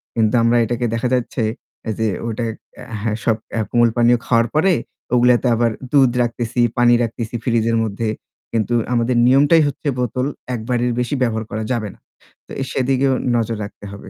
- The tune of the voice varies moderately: No, narrow, 1.7 semitones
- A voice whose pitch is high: No, low, 120 Hz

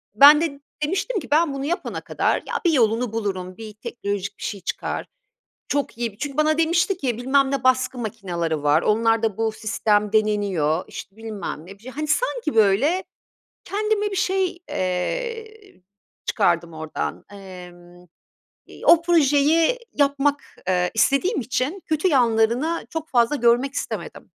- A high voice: Yes, high, 245 Hz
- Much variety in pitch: Yes, wide, 7.4 semitones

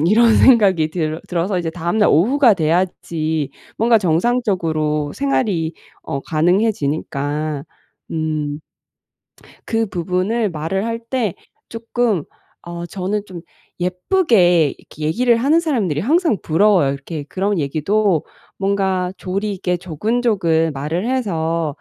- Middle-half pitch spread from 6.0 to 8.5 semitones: No, wide, 5.4 semitones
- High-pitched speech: No, medium, 180 Hz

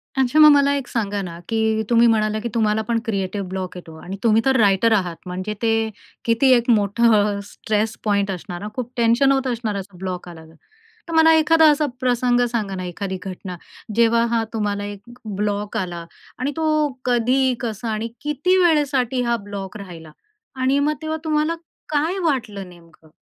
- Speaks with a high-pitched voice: Yes, high, 220 Hz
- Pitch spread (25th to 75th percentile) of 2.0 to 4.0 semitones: No, average, 4.4 semitones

